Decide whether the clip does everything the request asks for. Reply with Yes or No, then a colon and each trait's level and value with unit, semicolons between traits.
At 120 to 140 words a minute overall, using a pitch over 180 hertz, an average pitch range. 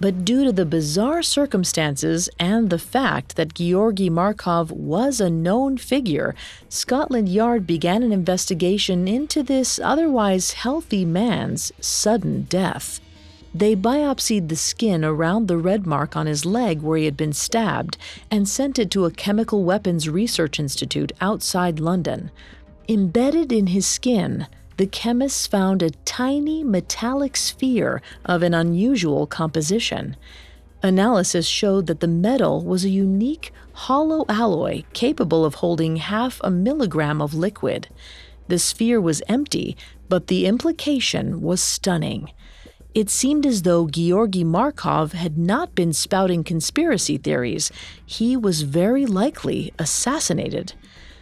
No: slow, 135 wpm; high, 190 Hz; wide, 5.8 semitones